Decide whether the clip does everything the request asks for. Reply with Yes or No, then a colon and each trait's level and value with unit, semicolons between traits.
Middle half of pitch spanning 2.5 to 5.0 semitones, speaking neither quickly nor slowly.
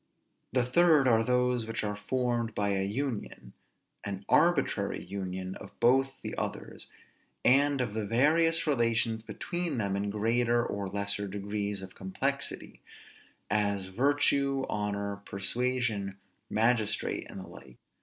No: average, 4.2 semitones; slow, 130 wpm